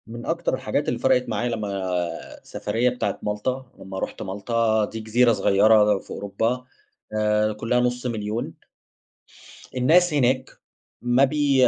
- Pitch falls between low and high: No, low, 115 Hz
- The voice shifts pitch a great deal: No, average, 2.8 semitones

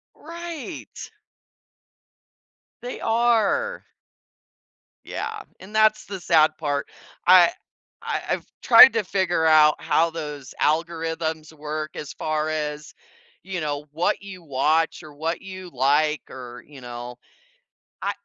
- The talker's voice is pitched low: No, medium, 160 Hz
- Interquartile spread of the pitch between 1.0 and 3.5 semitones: No, average, 3.9 semitones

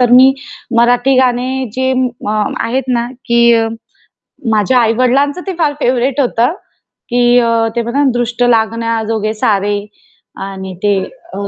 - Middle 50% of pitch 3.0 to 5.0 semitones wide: No, narrow, 2.5 semitones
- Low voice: No, high, 240 Hz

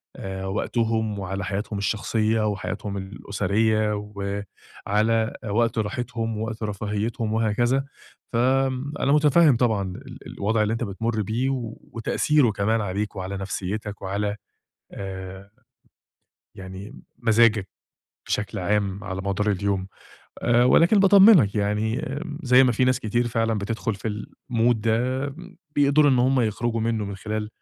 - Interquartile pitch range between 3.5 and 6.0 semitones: No, average, 3.0 semitones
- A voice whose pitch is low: Yes, low, 110 Hz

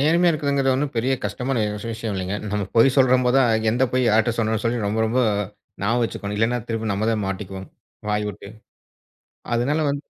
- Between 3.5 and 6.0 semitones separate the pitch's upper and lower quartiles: Yes, average, 3.8 semitones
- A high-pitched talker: No, low, 115 Hz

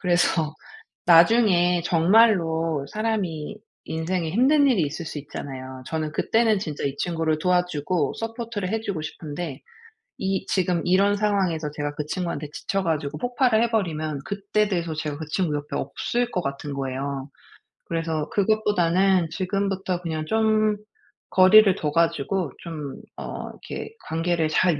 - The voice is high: No, medium, 175 Hz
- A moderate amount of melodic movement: Yes, average, 4.5 semitones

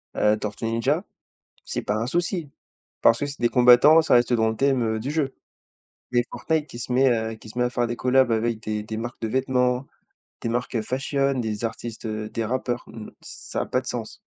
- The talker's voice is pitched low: Yes, low, 120 Hz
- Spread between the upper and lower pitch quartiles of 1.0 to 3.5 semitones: Yes, average, 2.9 semitones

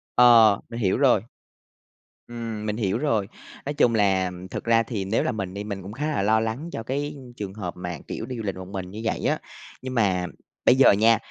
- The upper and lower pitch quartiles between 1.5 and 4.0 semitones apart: Yes, average, 3.4 semitones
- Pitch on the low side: Yes, low, 110 Hz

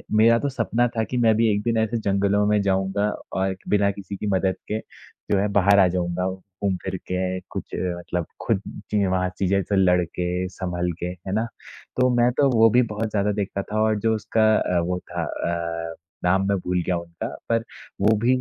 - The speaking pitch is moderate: No, low, 100 Hz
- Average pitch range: Yes, average, 3.0 semitones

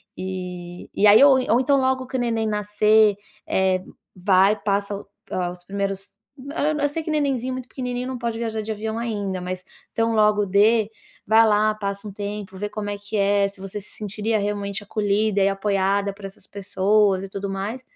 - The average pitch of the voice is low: No, high, 205 Hz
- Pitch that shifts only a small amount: Yes, narrow, 2.1 semitones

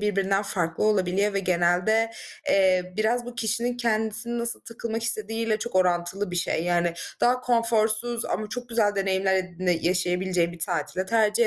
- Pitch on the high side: Yes, high, 205 Hz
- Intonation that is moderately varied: Yes, average, 4.0 semitones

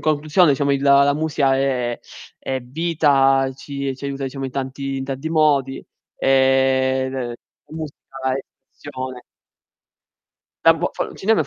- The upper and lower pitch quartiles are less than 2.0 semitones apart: Yes, narrow, 1.6 semitones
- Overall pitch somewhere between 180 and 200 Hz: No, low, 135 Hz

